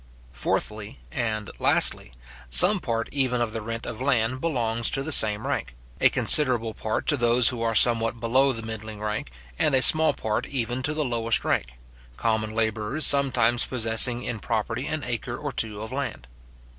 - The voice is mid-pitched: No, low, 115 Hz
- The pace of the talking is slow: No, average, 175 wpm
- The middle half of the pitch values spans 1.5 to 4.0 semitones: Yes, average, 2.8 semitones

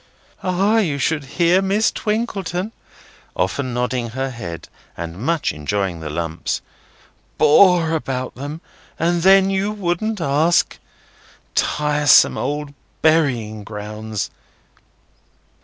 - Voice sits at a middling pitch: Yes, medium, 150 Hz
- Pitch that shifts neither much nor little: No, wide, 8.2 semitones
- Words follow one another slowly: Yes, slow, 105 wpm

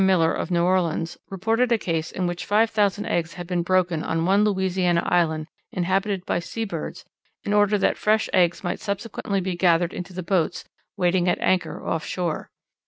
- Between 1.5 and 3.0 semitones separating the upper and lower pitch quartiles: Yes, narrow, 2.4 semitones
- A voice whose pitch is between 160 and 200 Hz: Yes, medium, 185 Hz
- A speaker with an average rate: Yes, average, 185 wpm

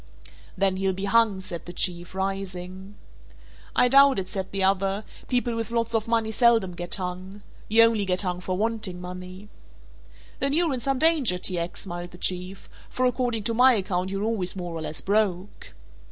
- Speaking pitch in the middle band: No, high, 195 Hz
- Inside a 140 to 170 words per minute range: No, average, 185 wpm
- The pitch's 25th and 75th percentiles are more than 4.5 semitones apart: No, average, 3.9 semitones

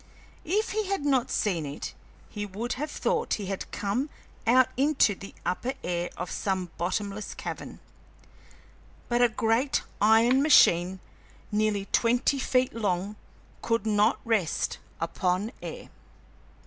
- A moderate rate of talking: No, slow, 130 wpm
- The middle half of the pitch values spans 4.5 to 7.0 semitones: Yes, average, 4.8 semitones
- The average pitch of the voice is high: Yes, high, 215 Hz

